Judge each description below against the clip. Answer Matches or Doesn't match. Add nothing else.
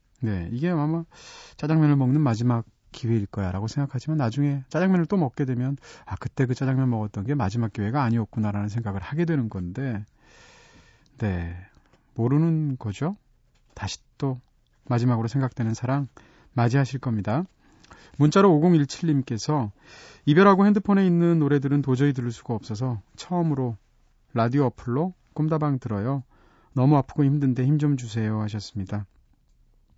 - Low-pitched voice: Matches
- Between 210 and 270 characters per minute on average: Doesn't match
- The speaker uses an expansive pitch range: Doesn't match